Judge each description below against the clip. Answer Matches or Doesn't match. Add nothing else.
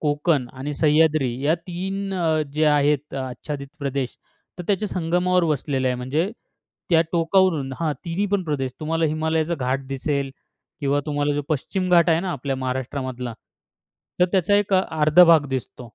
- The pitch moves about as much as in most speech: Matches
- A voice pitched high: Doesn't match